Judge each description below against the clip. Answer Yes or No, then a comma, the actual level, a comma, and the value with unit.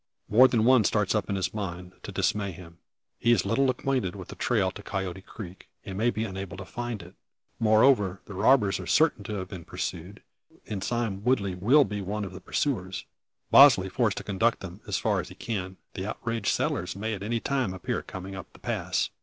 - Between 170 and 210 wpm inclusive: Yes, fast, 205 wpm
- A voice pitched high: No, low, 100 Hz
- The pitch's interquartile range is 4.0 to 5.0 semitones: No, average, 3.5 semitones